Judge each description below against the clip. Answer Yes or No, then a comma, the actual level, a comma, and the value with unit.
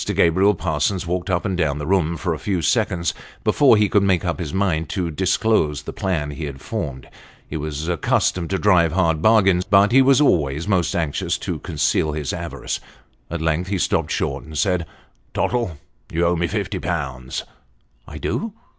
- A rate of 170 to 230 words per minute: Yes, average, 185 wpm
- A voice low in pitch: Yes, very low, 85 Hz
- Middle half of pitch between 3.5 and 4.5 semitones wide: Yes, average, 4.0 semitones